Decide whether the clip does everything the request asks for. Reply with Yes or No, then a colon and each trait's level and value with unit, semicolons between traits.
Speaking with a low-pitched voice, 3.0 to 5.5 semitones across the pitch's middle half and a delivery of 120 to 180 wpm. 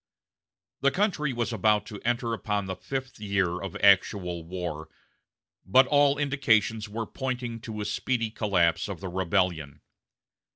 Yes: low, 105 Hz; average, 4.8 semitones; average, 140 wpm